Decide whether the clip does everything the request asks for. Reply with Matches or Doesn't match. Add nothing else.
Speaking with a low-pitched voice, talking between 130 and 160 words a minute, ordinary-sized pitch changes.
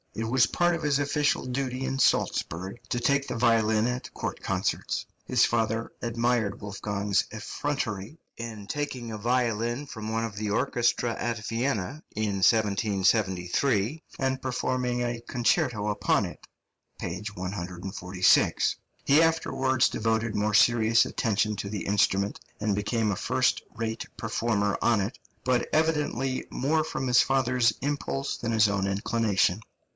Matches